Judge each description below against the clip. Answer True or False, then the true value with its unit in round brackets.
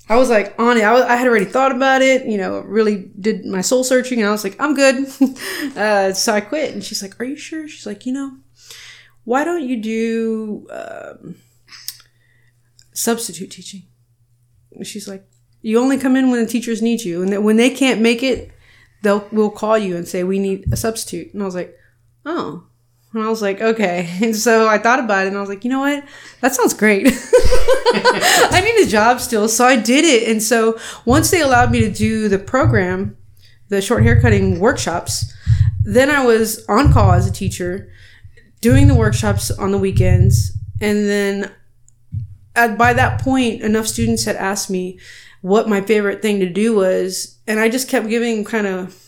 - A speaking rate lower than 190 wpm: False (200 wpm)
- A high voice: True (210 Hz)